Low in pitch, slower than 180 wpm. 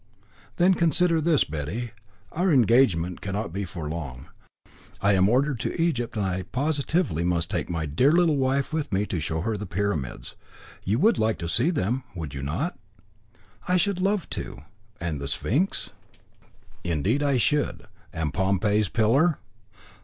Yes: low, 110 Hz; average, 160 wpm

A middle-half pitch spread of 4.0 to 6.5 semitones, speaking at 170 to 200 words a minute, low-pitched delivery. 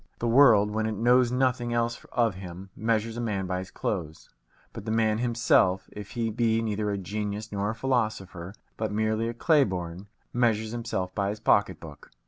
No: average, 2.8 semitones; average, 190 wpm; low, 110 Hz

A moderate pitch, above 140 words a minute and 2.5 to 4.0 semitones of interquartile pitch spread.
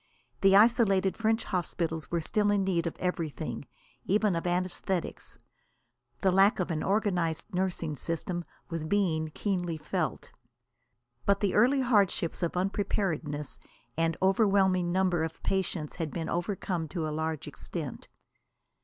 No: medium, 180 Hz; slow, 135 wpm; average, 3.2 semitones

